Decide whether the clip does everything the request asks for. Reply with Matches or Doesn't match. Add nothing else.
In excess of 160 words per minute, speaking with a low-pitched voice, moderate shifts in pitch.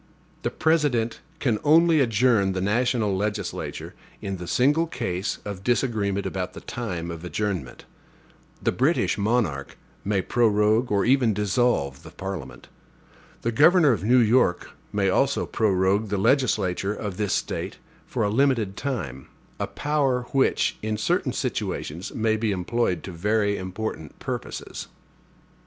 Doesn't match